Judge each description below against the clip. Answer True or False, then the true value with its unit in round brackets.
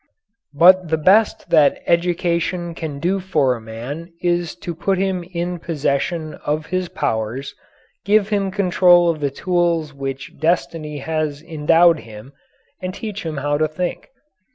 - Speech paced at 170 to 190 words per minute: False (155 wpm)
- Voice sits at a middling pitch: True (170 Hz)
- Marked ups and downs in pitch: False (3.4 semitones)